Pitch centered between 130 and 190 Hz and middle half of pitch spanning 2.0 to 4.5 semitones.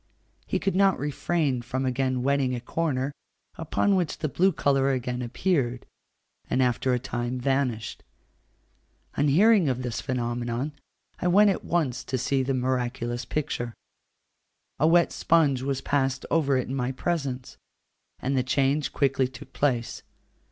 Yes: low, 135 Hz; average, 3.0 semitones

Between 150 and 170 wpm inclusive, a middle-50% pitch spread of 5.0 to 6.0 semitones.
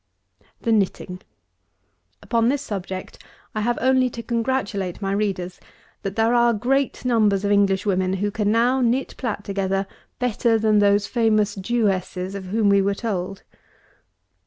No: average, 155 wpm; average, 3.2 semitones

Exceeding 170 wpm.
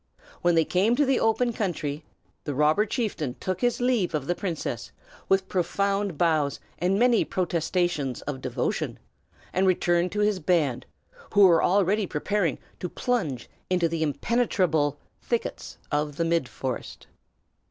No: average, 140 wpm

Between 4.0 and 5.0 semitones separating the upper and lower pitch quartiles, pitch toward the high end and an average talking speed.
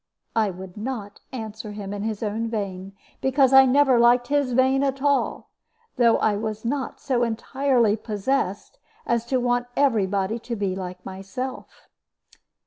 Yes: average, 4.3 semitones; high, 230 Hz; average, 155 wpm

